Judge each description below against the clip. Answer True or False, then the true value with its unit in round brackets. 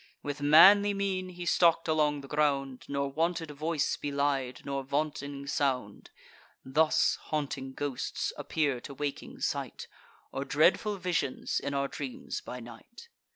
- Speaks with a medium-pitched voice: True (145 Hz)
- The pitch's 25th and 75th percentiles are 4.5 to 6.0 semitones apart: False (2.9 semitones)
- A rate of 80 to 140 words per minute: True (135 wpm)